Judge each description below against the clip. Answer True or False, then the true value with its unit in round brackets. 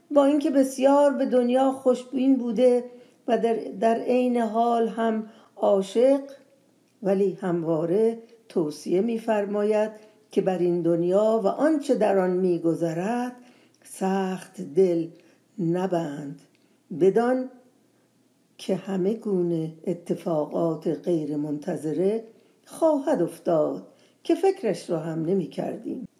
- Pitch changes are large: True (6.0 semitones)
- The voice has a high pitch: True (215 Hz)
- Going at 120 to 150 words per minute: False (105 wpm)